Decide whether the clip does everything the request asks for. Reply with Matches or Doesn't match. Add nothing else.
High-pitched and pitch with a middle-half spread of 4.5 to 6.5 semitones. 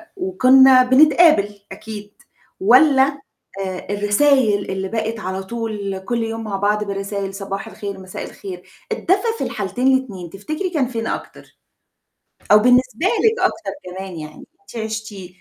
Matches